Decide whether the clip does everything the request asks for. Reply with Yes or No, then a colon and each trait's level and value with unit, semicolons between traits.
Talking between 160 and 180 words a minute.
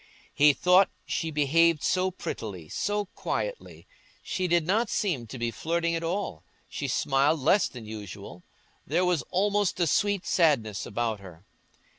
No: average, 150 wpm